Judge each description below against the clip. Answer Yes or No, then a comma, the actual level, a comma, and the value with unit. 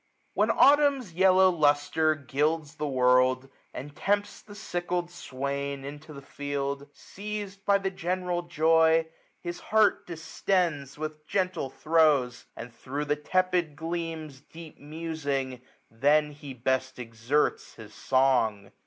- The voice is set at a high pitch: No, medium, 155 Hz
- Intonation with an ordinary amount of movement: Yes, average, 4.1 semitones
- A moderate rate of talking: No, slow, 130 wpm